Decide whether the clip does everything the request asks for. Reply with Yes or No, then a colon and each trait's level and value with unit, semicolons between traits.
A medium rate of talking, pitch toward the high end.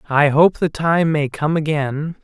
No: average, 190 wpm; medium, 155 Hz